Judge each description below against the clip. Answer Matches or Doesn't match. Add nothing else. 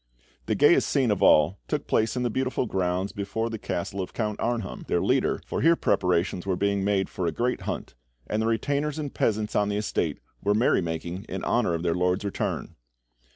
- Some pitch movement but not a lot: Matches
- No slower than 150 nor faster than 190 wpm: Doesn't match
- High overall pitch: Doesn't match